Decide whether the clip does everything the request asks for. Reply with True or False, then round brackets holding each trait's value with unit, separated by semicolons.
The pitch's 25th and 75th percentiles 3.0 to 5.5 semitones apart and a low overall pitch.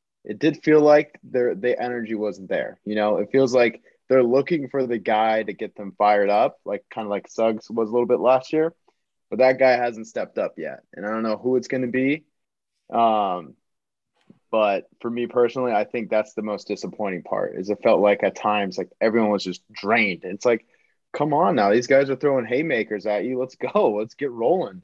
True (3.7 semitones; 120 Hz)